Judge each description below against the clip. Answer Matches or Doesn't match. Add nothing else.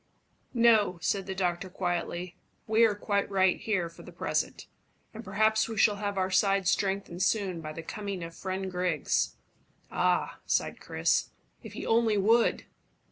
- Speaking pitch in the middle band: Doesn't match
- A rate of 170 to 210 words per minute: Doesn't match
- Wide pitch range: Doesn't match